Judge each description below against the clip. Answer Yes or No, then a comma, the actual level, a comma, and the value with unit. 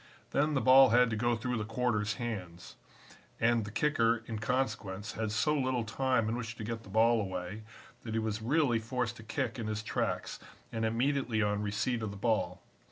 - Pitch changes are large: No, narrow, 2.5 semitones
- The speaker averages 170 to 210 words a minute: Yes, average, 200 wpm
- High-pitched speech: No, low, 115 Hz